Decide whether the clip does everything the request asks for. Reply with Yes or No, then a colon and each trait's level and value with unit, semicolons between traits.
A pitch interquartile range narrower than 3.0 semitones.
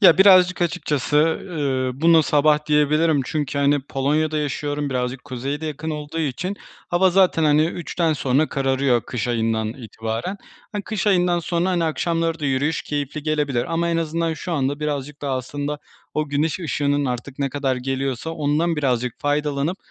No: average, 3.3 semitones